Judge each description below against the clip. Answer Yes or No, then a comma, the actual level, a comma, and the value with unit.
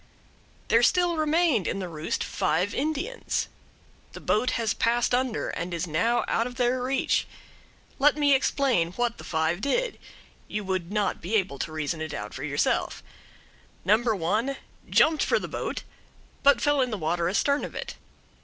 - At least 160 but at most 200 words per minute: Yes, average, 170 wpm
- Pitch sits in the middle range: No, high, 230 Hz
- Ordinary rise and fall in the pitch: No, wide, 7.9 semitones